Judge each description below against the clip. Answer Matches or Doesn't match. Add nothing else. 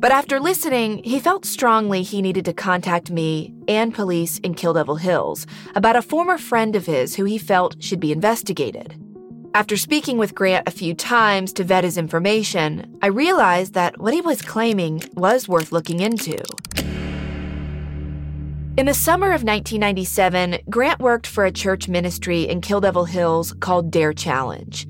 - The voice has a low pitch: Doesn't match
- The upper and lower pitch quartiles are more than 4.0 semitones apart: Matches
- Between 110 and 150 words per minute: Doesn't match